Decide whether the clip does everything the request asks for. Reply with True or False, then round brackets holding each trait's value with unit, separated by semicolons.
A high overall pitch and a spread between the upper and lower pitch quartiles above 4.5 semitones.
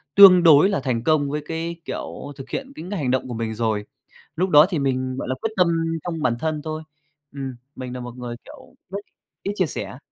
False (145 Hz; 5.0 semitones)